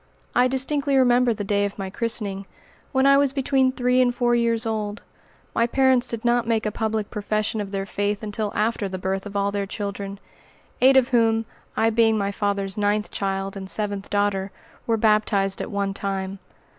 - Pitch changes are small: No, average, 3.2 semitones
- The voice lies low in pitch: No, high, 215 Hz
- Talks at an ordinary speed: Yes, average, 190 wpm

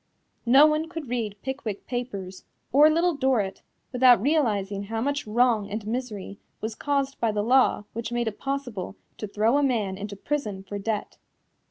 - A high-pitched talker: Yes, high, 235 Hz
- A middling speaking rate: Yes, average, 170 wpm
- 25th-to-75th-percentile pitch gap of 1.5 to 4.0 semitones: No, average, 4.7 semitones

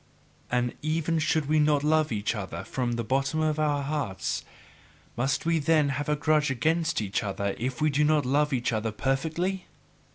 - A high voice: No, medium, 145 Hz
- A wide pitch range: No, average, 4.0 semitones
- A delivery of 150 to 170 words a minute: No, average, 185 wpm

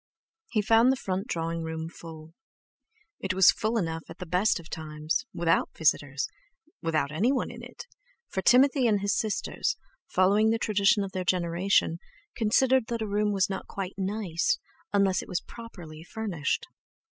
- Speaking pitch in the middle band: No, high, 195 Hz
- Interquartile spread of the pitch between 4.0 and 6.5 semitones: Yes, average, 5.1 semitones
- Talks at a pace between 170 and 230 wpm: No, average, 155 wpm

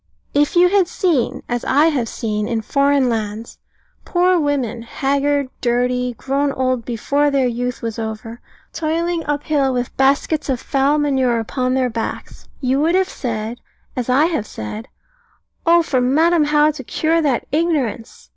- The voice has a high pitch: Yes, very high, 270 Hz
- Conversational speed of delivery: Yes, average, 160 wpm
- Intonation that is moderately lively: Yes, average, 3.8 semitones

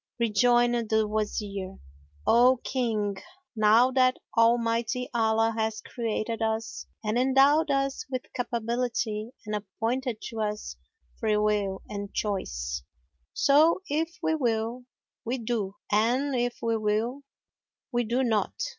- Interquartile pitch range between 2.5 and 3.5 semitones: Yes, average, 2.8 semitones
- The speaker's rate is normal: No, slow, 120 wpm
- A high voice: Yes, high, 230 Hz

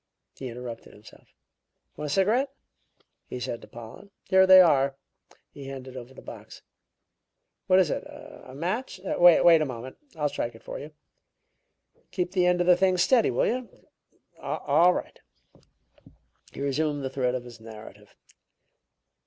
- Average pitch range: No, wide, 6.4 semitones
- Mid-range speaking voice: Yes, medium, 150 Hz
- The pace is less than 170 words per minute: Yes, average, 155 wpm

